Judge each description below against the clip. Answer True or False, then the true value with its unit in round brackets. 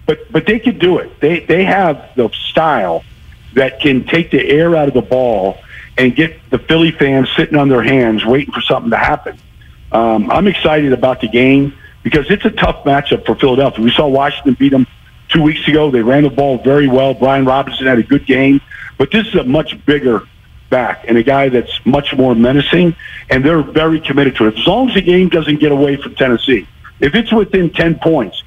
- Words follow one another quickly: True (215 wpm)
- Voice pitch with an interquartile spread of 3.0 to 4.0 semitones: True (3.6 semitones)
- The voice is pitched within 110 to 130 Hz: False (140 Hz)